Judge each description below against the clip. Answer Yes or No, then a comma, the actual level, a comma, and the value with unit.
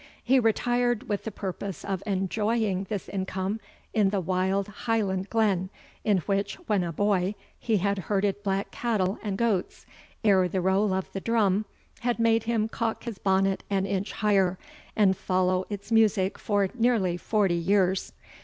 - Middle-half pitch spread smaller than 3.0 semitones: Yes, narrow, 2.5 semitones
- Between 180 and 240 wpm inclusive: No, average, 160 wpm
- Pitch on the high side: Yes, high, 200 Hz